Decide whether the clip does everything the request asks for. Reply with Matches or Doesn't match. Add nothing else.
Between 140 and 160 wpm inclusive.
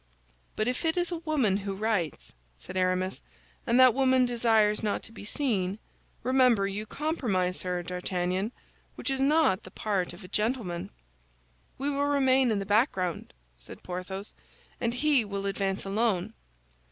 Matches